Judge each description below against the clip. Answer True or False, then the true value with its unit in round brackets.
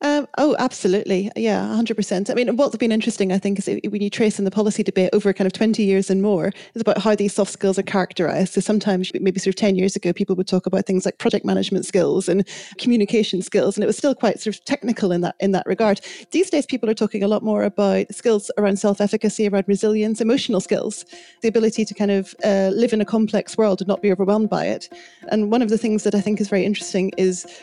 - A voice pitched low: False (205 Hz)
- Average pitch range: False (2.3 semitones)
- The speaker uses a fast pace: True (250 wpm)